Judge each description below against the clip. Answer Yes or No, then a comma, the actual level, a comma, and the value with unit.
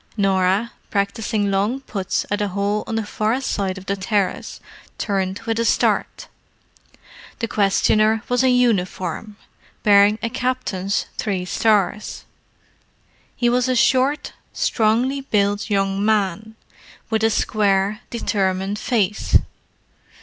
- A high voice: Yes, high, 210 Hz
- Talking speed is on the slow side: Yes, slow, 120 wpm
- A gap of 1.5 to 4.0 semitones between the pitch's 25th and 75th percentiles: Yes, narrow, 2.6 semitones